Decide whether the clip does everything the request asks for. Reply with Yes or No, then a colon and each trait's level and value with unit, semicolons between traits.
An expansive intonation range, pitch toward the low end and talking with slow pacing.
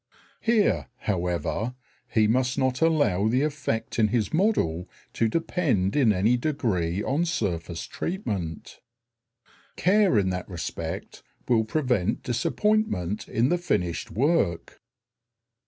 Yes: wide, 8.8 semitones; low, 115 Hz; slow, 115 wpm